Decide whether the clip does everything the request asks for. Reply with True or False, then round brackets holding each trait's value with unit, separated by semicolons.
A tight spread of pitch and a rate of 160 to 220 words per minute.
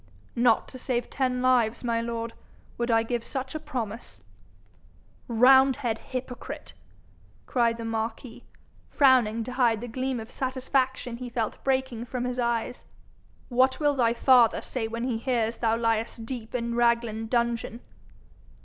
False (1.9 semitones; 145 wpm)